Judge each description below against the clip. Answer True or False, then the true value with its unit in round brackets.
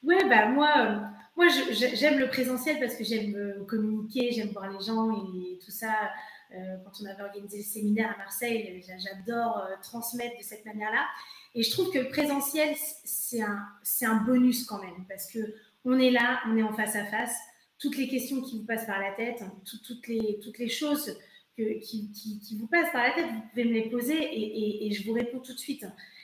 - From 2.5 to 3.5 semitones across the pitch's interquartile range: True (3.1 semitones)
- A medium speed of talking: False (230 wpm)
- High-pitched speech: True (225 Hz)